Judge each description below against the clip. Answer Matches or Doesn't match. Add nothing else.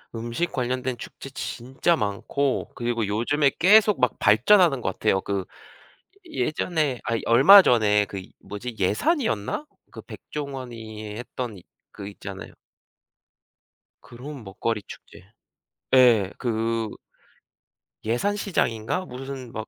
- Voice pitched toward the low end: Matches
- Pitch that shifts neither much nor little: Matches